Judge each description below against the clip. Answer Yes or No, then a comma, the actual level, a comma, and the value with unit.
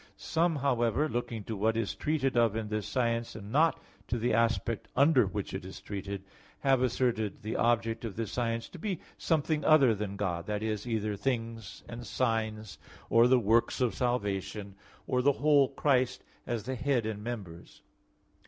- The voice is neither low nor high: No, low, 115 Hz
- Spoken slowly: No, average, 175 wpm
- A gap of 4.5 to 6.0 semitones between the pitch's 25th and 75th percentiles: No, average, 3.2 semitones